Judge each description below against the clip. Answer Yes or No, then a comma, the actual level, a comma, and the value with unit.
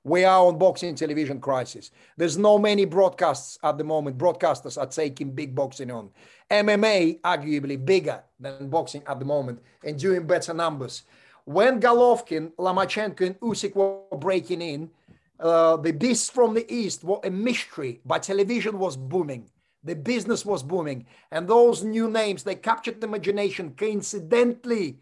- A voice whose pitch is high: No, medium, 180 Hz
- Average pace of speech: Yes, average, 155 wpm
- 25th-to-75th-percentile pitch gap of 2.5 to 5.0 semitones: No, wide, 5.4 semitones